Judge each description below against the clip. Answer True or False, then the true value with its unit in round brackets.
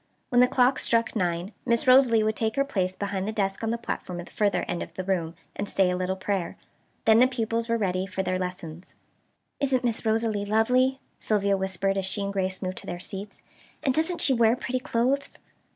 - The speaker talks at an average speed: False (215 wpm)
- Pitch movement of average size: True (3.8 semitones)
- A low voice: False (210 Hz)